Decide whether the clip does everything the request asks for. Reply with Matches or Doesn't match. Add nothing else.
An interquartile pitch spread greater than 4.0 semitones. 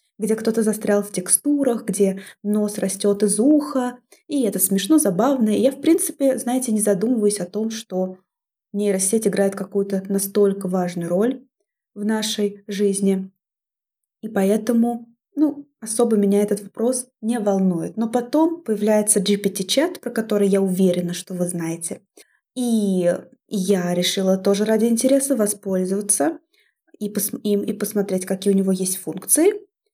Doesn't match